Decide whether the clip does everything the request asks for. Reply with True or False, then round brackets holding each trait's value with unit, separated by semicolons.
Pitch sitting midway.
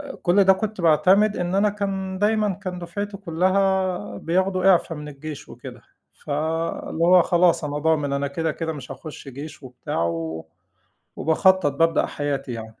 True (170 Hz)